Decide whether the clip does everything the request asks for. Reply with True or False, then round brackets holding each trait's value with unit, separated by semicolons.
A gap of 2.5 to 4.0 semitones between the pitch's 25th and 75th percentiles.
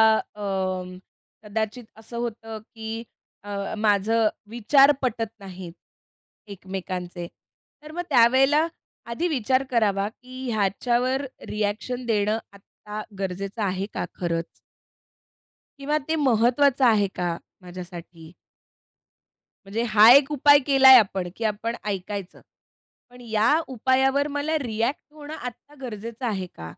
False (4.7 semitones)